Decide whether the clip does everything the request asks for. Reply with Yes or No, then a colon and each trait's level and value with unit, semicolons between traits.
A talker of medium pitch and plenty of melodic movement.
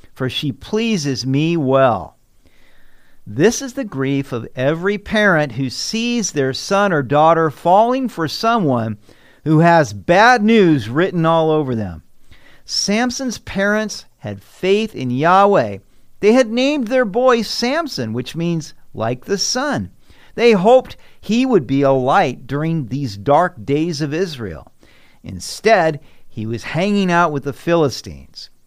Yes: medium, 160 Hz; wide, 8.0 semitones